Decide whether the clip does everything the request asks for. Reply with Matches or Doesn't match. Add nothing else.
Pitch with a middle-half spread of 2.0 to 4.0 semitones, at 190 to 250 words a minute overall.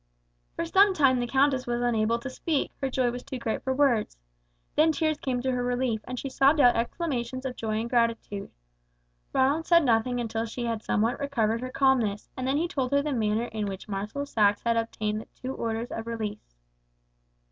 Matches